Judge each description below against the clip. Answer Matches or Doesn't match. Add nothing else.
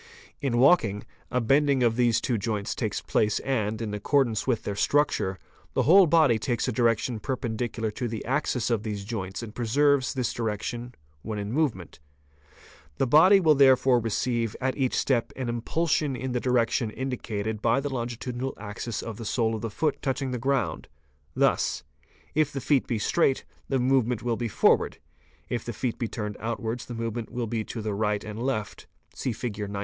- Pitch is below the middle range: Matches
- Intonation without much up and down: Doesn't match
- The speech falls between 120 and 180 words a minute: Doesn't match